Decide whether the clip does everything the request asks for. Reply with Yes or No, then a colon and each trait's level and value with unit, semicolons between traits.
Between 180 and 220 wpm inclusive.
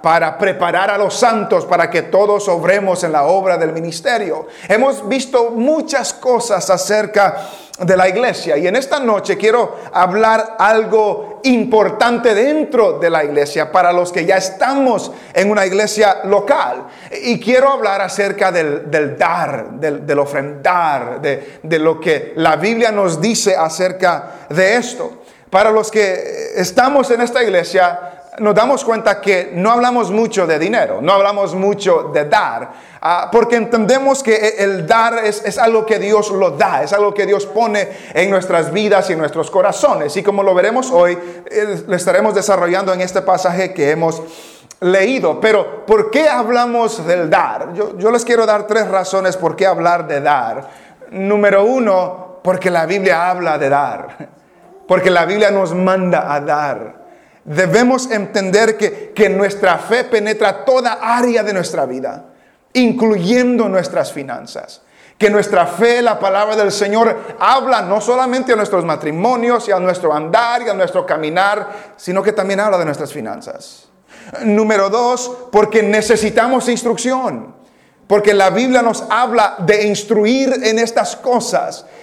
No: average, 155 wpm